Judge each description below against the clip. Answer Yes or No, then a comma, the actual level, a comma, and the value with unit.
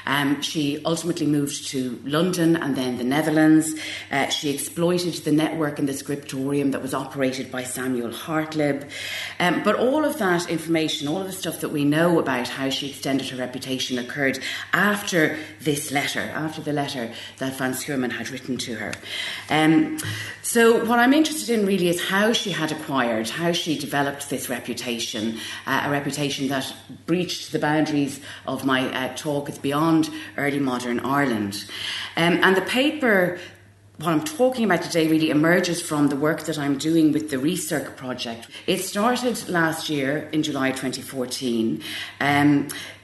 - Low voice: No, medium, 145 Hz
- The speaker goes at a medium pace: Yes, average, 165 wpm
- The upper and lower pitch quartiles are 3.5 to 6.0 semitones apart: Yes, average, 3.8 semitones